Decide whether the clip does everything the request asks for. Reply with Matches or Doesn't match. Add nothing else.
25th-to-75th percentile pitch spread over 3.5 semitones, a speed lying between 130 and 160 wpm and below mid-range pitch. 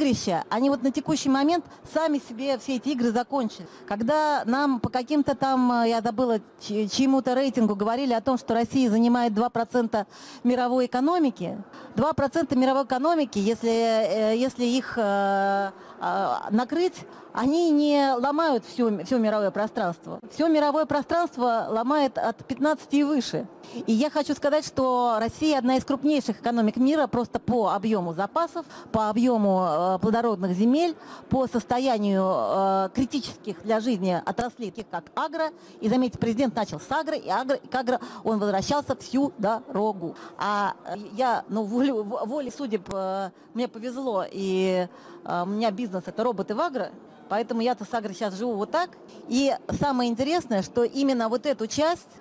Doesn't match